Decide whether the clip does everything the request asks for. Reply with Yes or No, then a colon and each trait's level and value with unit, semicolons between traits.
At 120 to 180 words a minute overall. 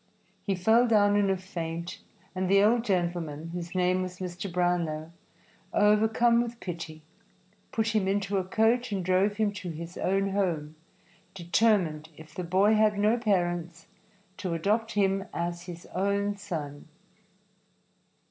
Yes: average, 145 wpm